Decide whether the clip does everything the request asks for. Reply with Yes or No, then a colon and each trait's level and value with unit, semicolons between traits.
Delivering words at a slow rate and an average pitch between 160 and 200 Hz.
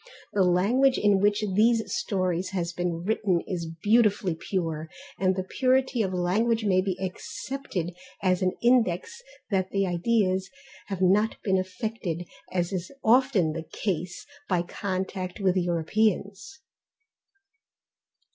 Yes: slow, 130 wpm; high, 190 Hz